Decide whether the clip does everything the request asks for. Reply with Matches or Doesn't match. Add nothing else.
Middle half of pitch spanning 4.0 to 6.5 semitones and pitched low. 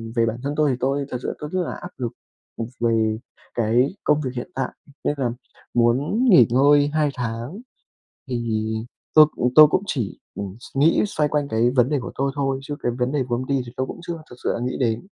Doesn't match